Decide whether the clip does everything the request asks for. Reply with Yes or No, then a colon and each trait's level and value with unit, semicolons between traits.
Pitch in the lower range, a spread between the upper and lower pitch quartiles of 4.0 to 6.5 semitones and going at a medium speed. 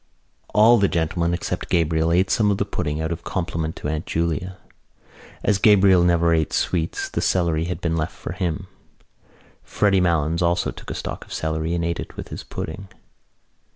No: very low, 85 Hz; narrow, 2.4 semitones; average, 185 wpm